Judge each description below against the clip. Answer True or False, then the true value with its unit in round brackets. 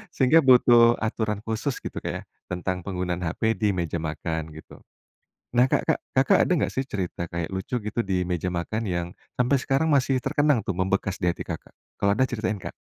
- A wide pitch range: True (5.9 semitones)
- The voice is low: True (105 Hz)